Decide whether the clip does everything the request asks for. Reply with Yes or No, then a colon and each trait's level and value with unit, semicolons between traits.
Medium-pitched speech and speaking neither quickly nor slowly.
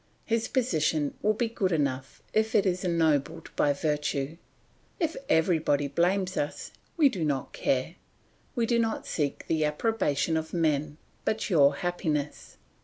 Yes: medium, 160 Hz; average, 145 wpm